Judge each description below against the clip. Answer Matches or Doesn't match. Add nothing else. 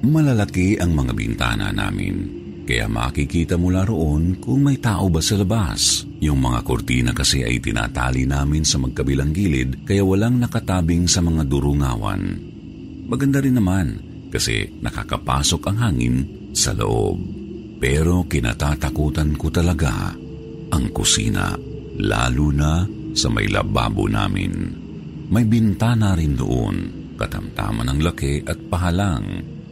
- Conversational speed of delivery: Matches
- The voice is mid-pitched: Doesn't match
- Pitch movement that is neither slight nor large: Doesn't match